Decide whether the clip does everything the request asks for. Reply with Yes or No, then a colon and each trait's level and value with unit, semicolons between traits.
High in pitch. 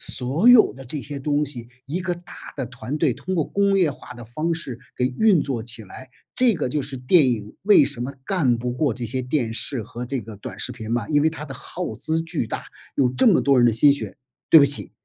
No: low, 135 Hz